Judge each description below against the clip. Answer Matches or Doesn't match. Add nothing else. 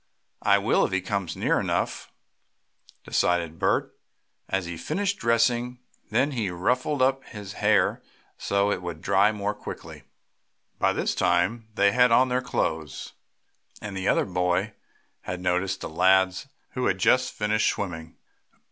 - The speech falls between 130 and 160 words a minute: Matches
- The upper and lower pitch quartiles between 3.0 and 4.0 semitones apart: Doesn't match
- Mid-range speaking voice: Doesn't match